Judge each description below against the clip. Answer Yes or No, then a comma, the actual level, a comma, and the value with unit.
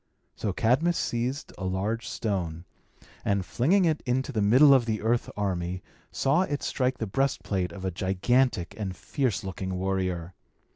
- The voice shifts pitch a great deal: Yes, wide, 5.7 semitones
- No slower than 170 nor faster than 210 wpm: No, average, 160 wpm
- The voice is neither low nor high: No, low, 110 Hz